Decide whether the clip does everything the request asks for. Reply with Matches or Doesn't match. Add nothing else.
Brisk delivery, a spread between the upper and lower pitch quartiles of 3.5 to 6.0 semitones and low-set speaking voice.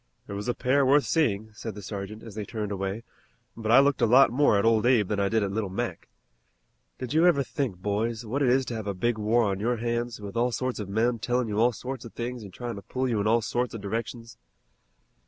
Doesn't match